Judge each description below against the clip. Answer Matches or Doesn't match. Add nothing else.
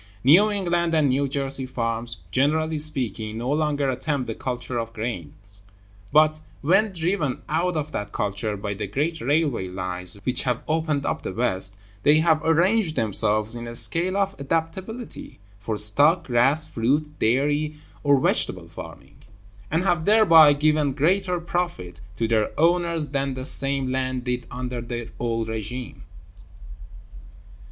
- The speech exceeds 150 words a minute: Doesn't match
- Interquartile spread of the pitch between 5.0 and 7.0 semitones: Matches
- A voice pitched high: Doesn't match